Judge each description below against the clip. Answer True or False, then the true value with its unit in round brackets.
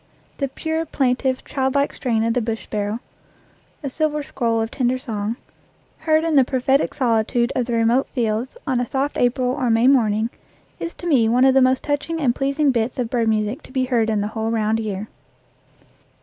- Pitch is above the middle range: True (250 Hz)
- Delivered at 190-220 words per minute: True (200 wpm)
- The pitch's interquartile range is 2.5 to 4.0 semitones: True (3.2 semitones)